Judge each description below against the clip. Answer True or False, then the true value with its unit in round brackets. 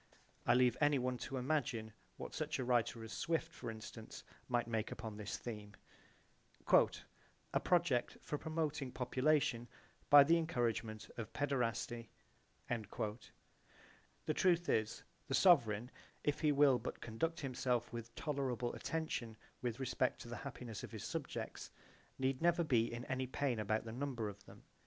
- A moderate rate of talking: True (150 wpm)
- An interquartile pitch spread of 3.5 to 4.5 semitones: True (3.9 semitones)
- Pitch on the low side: True (125 Hz)